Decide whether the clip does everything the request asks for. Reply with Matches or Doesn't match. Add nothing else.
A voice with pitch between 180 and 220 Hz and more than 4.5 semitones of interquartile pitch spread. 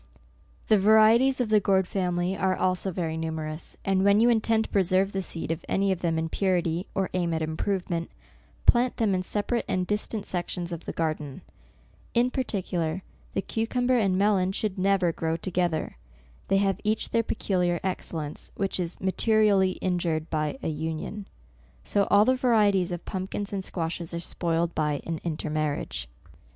Doesn't match